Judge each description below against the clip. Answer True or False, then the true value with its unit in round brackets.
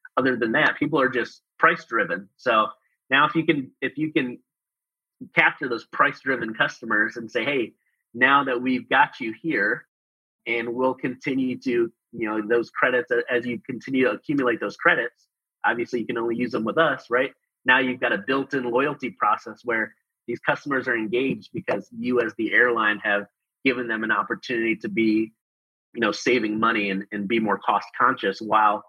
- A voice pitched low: True (120 Hz)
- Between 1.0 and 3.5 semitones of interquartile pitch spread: True (2.8 semitones)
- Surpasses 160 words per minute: True (185 wpm)